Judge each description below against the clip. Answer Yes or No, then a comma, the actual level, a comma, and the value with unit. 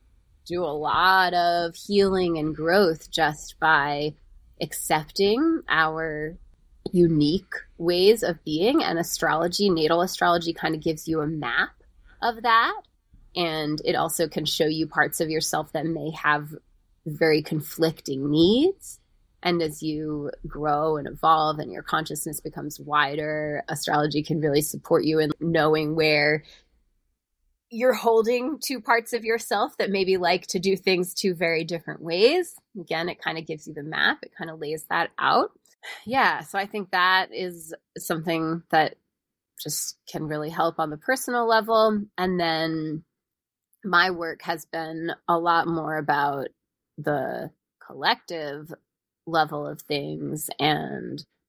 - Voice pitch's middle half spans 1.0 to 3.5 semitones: Yes, average, 2.8 semitones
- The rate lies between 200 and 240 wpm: No, average, 145 wpm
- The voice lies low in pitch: No, medium, 160 Hz